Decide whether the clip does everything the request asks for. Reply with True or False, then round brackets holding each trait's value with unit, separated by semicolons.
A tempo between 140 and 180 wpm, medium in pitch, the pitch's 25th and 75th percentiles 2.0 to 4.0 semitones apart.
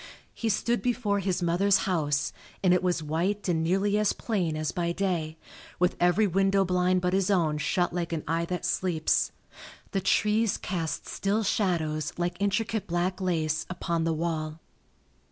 True (165 wpm; 180 Hz; 3.1 semitones)